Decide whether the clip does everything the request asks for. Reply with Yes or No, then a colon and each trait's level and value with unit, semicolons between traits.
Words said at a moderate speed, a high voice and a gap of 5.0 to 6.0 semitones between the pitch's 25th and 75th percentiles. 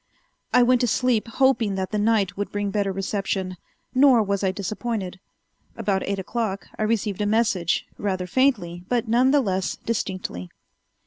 No: average, 165 wpm; high, 205 Hz; average, 3.4 semitones